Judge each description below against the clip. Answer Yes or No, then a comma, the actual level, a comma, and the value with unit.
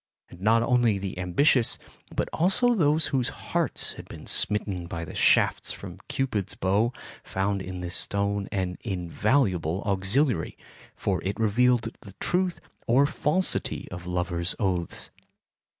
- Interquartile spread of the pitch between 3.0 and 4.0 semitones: No, wide, 5.4 semitones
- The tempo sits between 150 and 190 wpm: No, slow, 135 wpm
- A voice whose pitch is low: Yes, low, 100 Hz